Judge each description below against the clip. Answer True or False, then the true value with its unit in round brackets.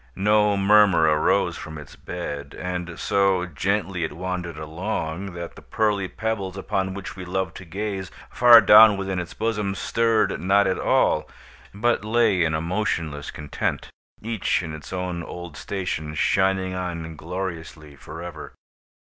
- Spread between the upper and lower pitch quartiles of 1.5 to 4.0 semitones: True (3.3 semitones)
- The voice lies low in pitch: True (95 Hz)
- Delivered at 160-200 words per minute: False (145 wpm)